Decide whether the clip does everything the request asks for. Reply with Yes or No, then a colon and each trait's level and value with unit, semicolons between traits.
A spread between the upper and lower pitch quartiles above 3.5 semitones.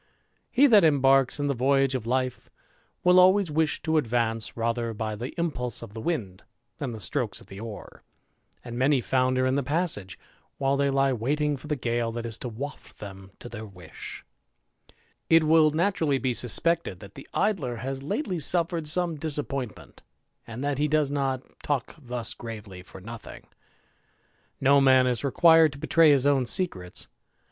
Yes: average, 4.5 semitones